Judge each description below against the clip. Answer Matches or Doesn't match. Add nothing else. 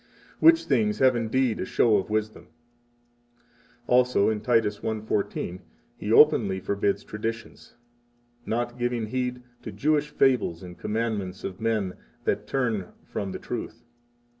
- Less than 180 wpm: Matches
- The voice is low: Matches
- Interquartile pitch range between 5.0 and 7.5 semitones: Doesn't match